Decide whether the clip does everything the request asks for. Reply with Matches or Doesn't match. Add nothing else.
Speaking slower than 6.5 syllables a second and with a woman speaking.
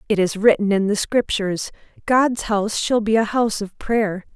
Matches